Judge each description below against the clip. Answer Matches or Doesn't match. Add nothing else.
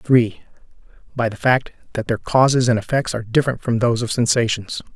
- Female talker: Doesn't match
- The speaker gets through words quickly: Doesn't match